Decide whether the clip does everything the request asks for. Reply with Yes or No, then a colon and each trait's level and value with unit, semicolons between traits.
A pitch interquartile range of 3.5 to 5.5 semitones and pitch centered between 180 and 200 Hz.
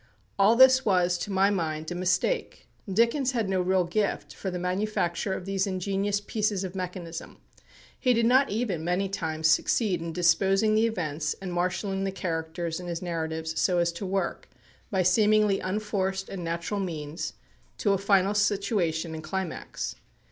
No: average, 3.0 semitones; high, 190 Hz